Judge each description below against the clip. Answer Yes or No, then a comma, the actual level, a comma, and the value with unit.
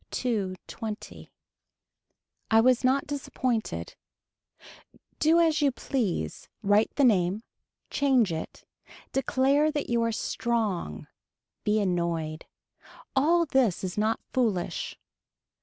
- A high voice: Yes, high, 230 Hz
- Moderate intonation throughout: No, wide, 5.9 semitones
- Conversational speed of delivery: No, slow, 105 wpm